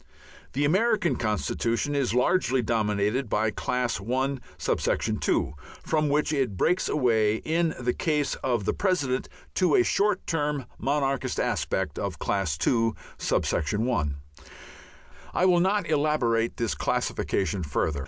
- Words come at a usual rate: No, slow, 120 wpm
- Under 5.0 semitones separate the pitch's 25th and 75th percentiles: No, wide, 5.4 semitones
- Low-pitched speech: Yes, low, 130 Hz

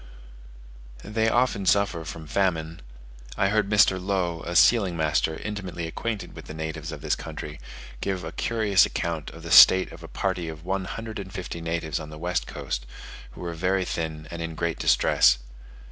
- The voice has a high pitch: No, very low, 85 Hz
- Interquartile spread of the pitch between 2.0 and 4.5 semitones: Yes, average, 3.5 semitones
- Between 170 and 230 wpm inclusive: Yes, average, 180 wpm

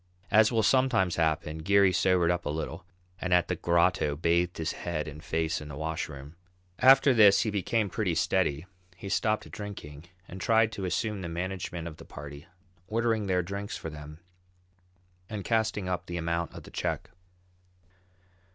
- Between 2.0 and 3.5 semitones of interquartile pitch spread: No, average, 4.2 semitones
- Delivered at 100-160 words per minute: No, average, 170 wpm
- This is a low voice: Yes, very low, 90 Hz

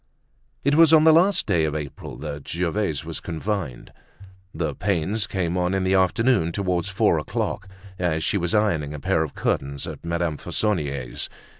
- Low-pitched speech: Yes, very low, 90 Hz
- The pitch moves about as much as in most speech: Yes, average, 4.7 semitones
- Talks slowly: No, average, 170 wpm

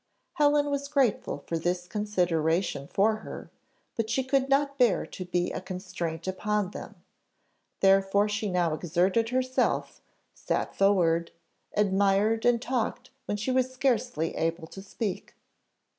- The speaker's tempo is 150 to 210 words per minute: No, slow, 135 wpm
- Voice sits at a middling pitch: No, high, 200 Hz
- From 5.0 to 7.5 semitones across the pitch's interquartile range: Yes, wide, 5.4 semitones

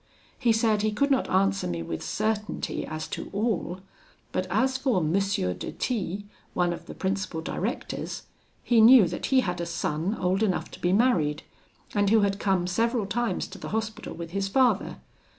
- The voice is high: Yes, high, 200 Hz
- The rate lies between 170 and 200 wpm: Yes, average, 185 wpm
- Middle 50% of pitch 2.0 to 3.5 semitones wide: No, average, 3.9 semitones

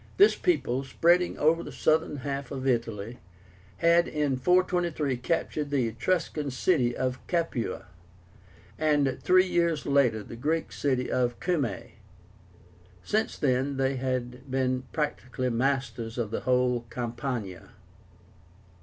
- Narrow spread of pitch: No, average, 4.1 semitones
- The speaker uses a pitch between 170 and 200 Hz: No, low, 135 Hz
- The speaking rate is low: Yes, slow, 125 wpm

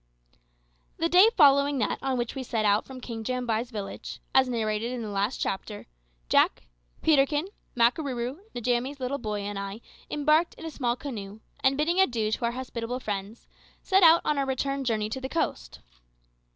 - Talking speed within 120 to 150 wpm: No, average, 175 wpm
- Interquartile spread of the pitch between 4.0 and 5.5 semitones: Yes, average, 4.3 semitones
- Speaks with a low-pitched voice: No, very high, 250 Hz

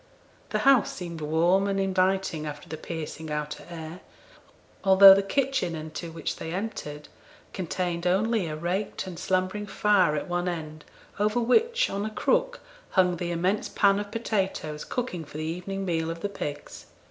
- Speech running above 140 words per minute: Yes, average, 165 wpm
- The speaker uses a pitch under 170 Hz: No, medium, 180 Hz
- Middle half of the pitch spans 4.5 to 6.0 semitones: No, average, 3.7 semitones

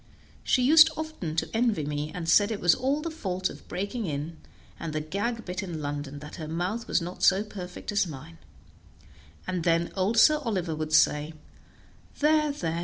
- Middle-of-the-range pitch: Yes, medium, 180 Hz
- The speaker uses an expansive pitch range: Yes, wide, 6.4 semitones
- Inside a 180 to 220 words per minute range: Yes, average, 185 wpm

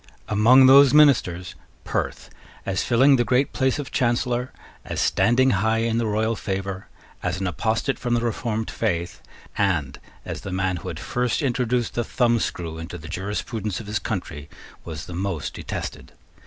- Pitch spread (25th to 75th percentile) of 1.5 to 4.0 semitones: No, average, 4.8 semitones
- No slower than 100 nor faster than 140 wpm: No, average, 165 wpm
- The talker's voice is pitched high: No, low, 110 Hz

